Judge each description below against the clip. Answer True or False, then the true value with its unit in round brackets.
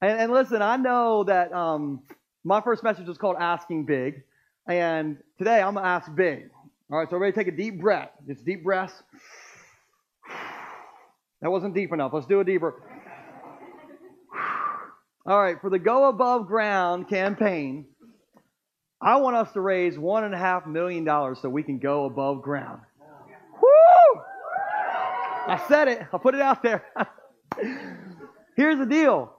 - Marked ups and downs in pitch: True (6.1 semitones)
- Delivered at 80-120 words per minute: False (155 wpm)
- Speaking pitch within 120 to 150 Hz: False (195 Hz)